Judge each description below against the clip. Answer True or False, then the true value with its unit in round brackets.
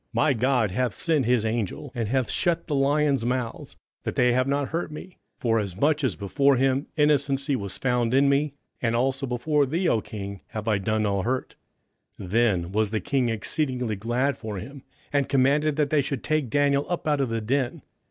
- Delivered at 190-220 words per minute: True (200 wpm)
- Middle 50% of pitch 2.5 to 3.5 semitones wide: False (4.0 semitones)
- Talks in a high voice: False (130 Hz)